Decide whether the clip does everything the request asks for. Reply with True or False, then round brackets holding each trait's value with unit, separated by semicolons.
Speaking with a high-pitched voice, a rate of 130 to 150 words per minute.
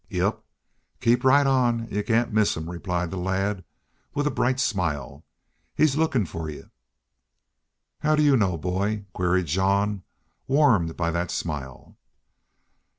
False (100 Hz; 145 wpm)